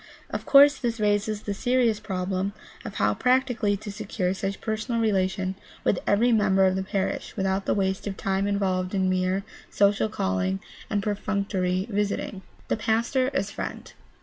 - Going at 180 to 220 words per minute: No, average, 160 wpm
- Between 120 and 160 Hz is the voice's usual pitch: No, high, 200 Hz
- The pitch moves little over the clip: Yes, narrow, 2.3 semitones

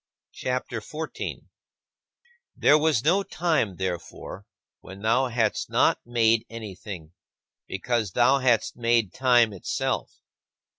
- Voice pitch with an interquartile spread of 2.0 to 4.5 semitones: Yes, average, 4.0 semitones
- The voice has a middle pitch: No, low, 115 Hz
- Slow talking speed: Yes, slow, 110 wpm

